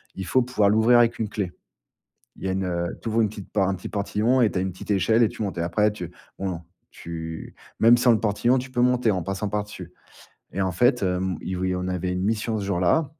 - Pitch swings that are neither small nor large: Yes, average, 3.6 semitones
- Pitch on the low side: Yes, low, 100 Hz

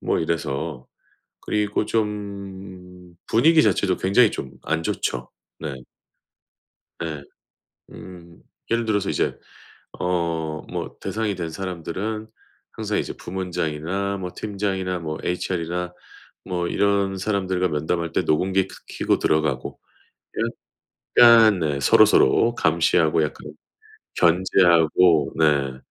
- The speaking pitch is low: Yes, very low, 90 Hz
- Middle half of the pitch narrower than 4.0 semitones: Yes, average, 3.5 semitones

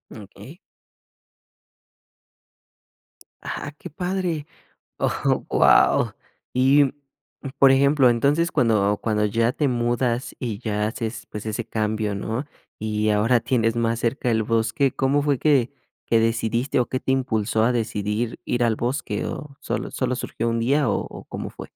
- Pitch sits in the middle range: No, low, 120 Hz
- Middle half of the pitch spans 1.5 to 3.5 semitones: Yes, average, 3.2 semitones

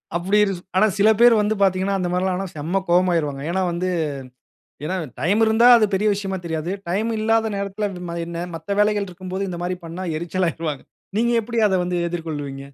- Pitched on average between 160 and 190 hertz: Yes, medium, 185 Hz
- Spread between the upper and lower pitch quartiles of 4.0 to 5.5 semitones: No, average, 3.2 semitones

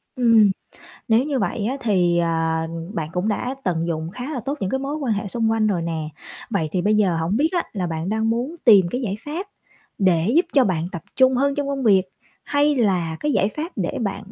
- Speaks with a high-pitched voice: Yes, high, 215 Hz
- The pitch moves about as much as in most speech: No, wide, 6.9 semitones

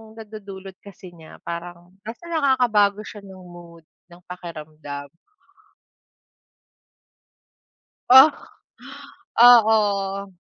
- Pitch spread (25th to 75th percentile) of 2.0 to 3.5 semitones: No, average, 3.9 semitones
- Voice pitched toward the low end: No, high, 195 Hz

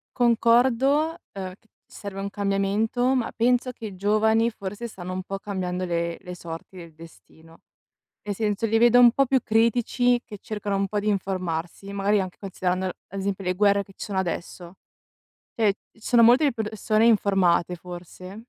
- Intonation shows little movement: No, average, 3.6 semitones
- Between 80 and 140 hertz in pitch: No, high, 200 Hz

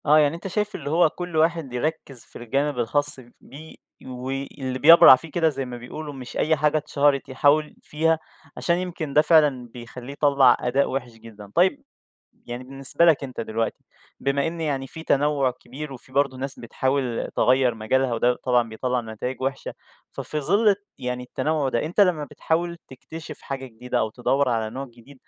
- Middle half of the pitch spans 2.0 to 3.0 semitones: No, average, 3.7 semitones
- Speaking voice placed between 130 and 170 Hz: Yes, low, 135 Hz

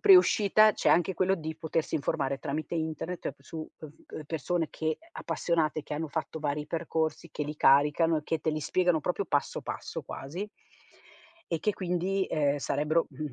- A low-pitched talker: No, medium, 160 Hz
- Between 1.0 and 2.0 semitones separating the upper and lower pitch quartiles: No, narrow, 2.6 semitones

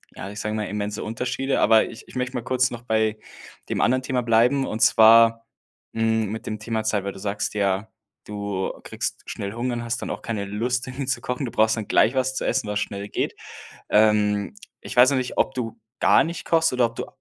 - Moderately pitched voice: No, low, 115 Hz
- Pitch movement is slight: No, average, 3.1 semitones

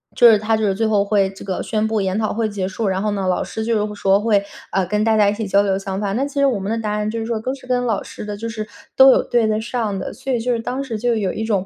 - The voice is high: Yes, high, 215 Hz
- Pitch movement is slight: Yes, narrow, 2.3 semitones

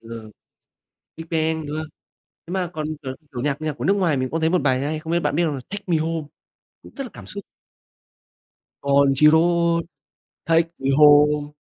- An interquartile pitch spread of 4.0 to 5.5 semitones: No, narrow, 2.5 semitones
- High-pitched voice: No, medium, 155 Hz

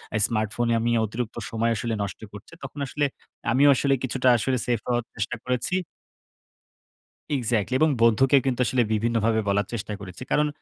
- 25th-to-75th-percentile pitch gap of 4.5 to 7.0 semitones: No, average, 3.0 semitones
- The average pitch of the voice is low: Yes, low, 120 Hz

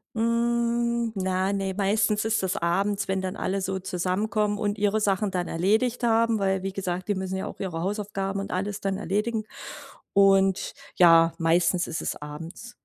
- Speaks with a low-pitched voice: No, high, 195 Hz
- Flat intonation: Yes, narrow, 2.3 semitones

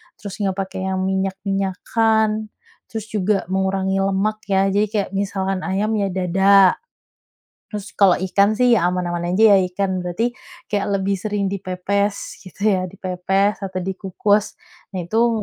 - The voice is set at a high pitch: Yes, high, 195 Hz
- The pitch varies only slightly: Yes, narrow, 1.5 semitones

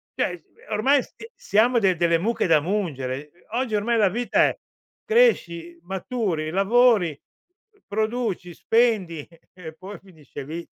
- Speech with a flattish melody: No, wide, 5.6 semitones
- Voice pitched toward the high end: Yes, high, 195 Hz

